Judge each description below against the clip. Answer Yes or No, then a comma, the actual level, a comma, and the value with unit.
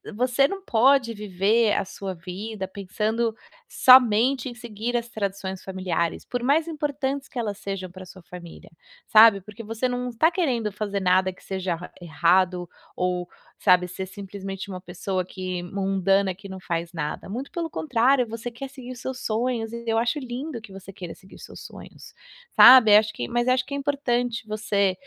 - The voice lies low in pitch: No, high, 215 Hz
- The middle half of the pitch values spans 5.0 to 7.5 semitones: No, average, 4.6 semitones